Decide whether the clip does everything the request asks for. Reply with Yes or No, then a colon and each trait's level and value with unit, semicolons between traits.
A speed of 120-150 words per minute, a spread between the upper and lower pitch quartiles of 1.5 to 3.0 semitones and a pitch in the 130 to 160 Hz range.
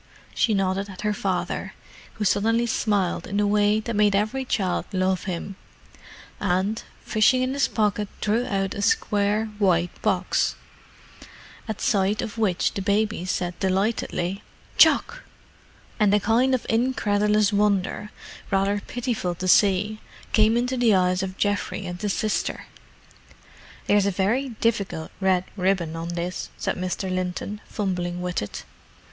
No: average, 140 wpm; narrow, 2.6 semitones; high, 205 Hz